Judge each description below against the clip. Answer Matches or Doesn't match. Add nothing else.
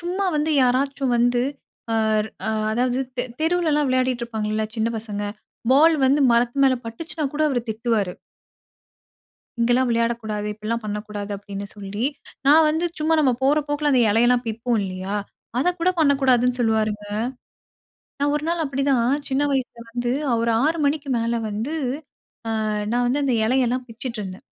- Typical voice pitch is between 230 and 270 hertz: Matches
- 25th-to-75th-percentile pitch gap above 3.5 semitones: Matches